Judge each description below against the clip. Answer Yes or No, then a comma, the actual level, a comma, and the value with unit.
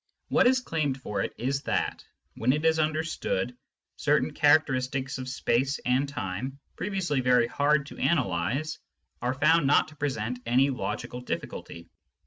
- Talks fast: No, average, 145 wpm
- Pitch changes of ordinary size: Yes, average, 3.4 semitones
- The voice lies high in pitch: No, low, 135 Hz